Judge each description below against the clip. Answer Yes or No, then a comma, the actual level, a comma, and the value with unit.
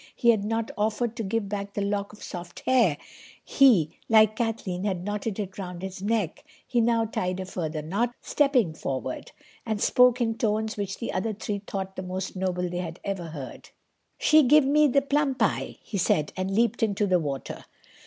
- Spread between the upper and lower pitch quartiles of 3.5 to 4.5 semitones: Yes, average, 3.8 semitones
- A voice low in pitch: No, high, 205 Hz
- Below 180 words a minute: No, average, 195 wpm